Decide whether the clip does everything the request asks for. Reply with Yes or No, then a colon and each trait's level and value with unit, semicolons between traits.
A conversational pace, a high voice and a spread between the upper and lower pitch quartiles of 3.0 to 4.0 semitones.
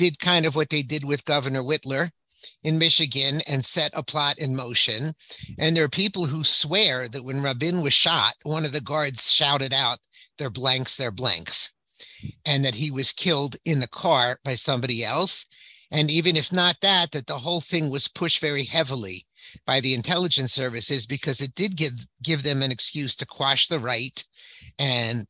No: average, 185 wpm; medium, 145 Hz; average, 3.3 semitones